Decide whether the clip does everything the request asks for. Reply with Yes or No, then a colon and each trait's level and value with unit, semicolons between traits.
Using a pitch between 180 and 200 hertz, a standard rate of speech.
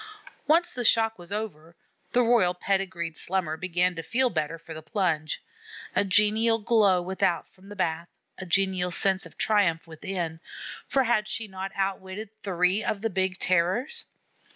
Yes: high, 190 Hz; average, 160 wpm